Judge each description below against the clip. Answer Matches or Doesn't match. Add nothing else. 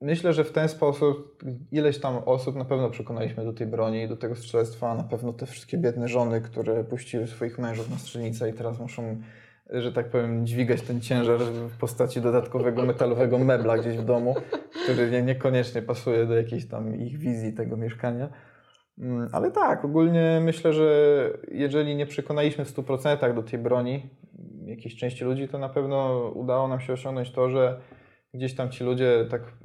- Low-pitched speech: Matches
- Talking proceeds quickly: Matches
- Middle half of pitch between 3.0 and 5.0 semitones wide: Doesn't match